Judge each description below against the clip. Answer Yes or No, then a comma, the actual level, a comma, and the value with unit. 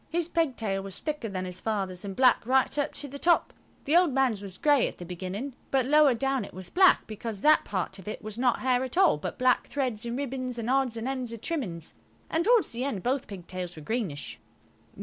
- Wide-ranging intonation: Yes, wide, 5.7 semitones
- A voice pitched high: Yes, high, 245 Hz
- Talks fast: Yes, fast, 230 wpm